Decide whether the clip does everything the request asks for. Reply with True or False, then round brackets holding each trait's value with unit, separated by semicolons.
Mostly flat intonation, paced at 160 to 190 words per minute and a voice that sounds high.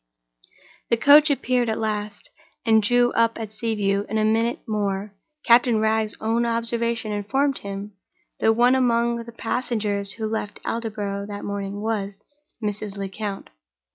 False (2.3 semitones; 140 wpm; 220 Hz)